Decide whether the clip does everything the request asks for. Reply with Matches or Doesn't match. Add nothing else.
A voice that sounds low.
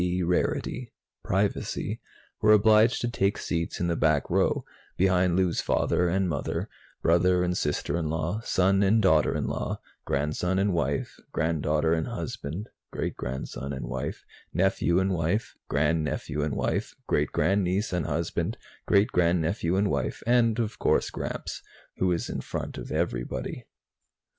Matches